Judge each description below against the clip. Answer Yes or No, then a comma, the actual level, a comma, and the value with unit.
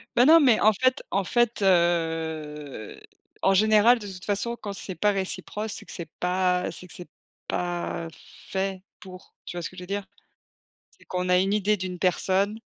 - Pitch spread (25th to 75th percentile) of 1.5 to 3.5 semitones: Yes, average, 2.8 semitones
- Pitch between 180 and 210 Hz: Yes, high, 190 Hz